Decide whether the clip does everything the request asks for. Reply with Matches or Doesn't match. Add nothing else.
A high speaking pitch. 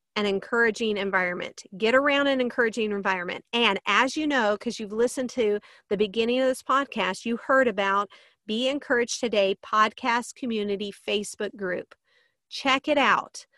Matches